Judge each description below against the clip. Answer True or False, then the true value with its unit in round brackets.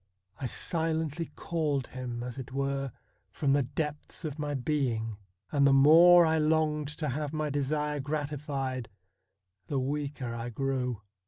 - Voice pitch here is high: False (145 Hz)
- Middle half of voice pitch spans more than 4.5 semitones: False (2.6 semitones)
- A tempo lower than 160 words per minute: True (145 wpm)